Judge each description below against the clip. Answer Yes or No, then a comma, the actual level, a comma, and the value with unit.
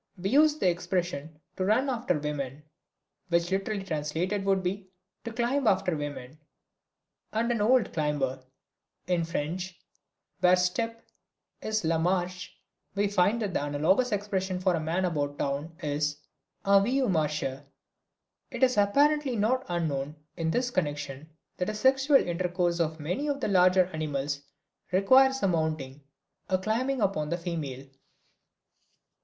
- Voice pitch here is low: No, medium, 180 Hz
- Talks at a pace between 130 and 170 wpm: Yes, average, 140 wpm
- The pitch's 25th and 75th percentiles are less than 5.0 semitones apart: No, wide, 5.5 semitones